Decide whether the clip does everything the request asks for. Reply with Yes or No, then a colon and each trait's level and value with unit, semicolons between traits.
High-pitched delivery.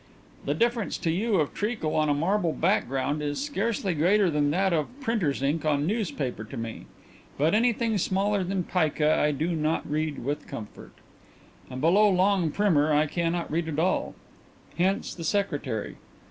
No: medium, 165 Hz